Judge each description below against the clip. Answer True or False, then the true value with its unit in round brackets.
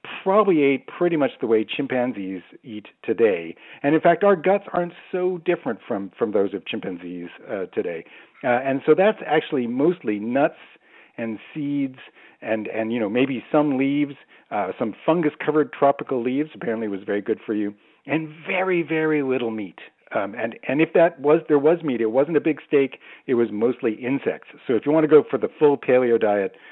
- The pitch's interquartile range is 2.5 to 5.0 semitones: False (5.6 semitones)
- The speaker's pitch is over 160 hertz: False (140 Hz)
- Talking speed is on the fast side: False (190 wpm)